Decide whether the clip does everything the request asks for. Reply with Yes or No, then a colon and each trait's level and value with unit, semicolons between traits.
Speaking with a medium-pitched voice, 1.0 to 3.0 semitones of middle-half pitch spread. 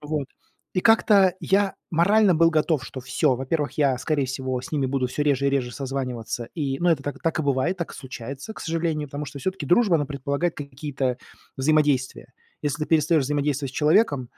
No: medium, 145 Hz; average, 3.6 semitones